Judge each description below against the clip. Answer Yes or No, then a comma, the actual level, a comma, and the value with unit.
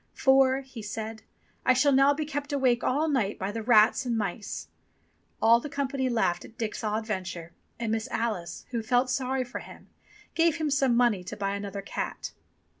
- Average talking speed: Yes, average, 190 wpm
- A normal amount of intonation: Yes, average, 4.0 semitones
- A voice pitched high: Yes, high, 240 Hz